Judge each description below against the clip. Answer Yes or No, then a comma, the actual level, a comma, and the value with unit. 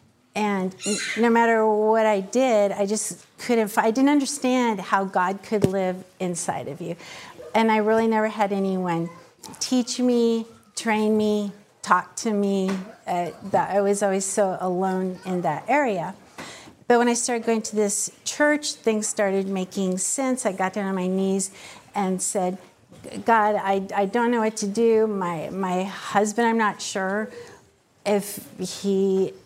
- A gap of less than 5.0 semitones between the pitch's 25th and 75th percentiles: Yes, average, 2.9 semitones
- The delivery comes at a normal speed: Yes, average, 160 wpm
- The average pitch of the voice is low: No, high, 205 Hz